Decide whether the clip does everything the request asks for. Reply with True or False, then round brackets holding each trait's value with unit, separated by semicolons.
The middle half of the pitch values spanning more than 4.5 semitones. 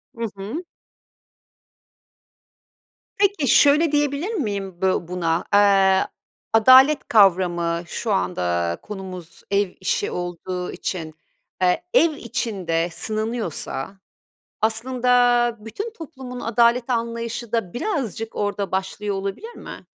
True (5.0 semitones)